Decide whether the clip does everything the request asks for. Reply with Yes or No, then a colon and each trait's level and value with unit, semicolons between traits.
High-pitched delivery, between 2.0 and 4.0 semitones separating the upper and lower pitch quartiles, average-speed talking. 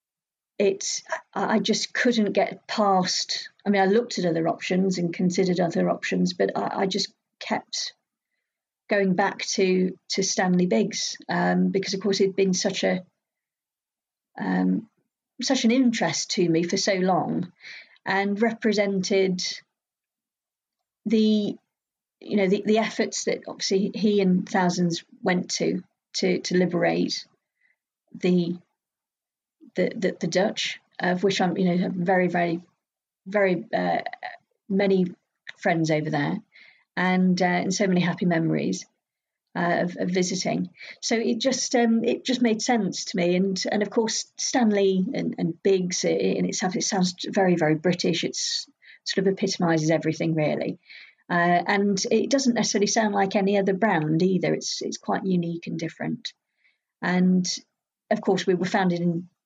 Yes: high, 195 Hz; average, 3.2 semitones; average, 150 wpm